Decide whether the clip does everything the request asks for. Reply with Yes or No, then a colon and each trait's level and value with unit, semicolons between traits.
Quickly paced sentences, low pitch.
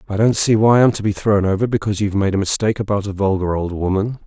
Yes: fast, 265 wpm; low, 100 Hz